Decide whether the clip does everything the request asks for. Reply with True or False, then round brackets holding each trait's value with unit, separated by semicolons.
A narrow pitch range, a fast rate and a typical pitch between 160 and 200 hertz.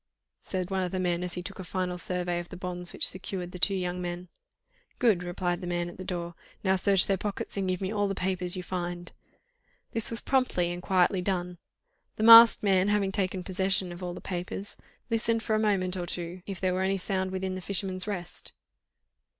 True (1.6 semitones; 215 wpm; 185 Hz)